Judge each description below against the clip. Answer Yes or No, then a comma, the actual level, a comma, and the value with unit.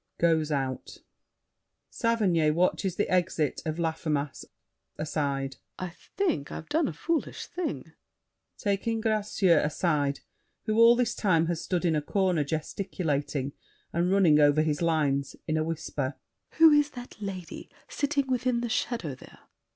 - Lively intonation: Yes, wide, 6.2 semitones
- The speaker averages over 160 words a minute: No, average, 140 wpm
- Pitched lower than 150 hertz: No, medium, 170 Hz